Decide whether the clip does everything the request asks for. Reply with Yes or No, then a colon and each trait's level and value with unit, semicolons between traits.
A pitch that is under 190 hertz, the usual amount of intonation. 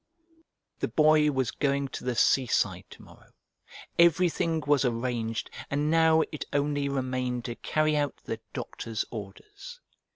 Yes: medium, 140 Hz; average, 3.7 semitones